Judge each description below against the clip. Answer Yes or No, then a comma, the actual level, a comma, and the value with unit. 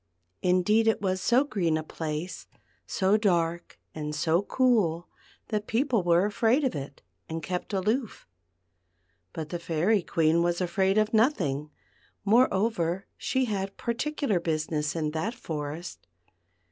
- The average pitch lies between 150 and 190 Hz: Yes, medium, 185 Hz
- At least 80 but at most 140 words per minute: Yes, slow, 135 wpm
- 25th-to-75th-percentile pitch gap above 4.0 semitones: Yes, average, 5.2 semitones